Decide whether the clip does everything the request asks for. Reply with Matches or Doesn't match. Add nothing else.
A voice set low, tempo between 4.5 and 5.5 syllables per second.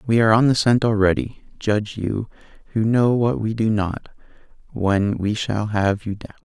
Matches